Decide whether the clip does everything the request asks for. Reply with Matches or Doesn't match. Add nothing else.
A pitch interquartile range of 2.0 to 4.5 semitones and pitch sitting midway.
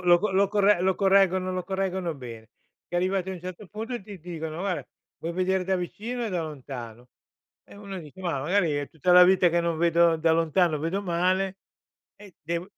Matches